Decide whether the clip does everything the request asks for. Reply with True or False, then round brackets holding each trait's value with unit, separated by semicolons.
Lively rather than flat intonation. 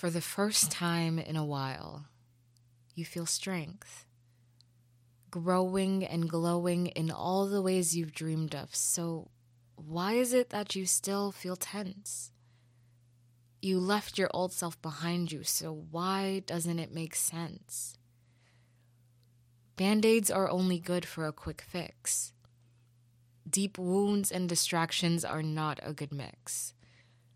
True (7.1 semitones)